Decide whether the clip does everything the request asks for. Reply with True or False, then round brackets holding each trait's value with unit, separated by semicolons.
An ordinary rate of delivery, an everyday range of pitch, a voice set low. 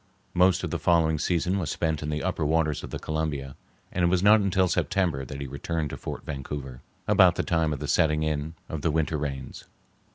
False (220 wpm; 3.0 semitones; 80 Hz)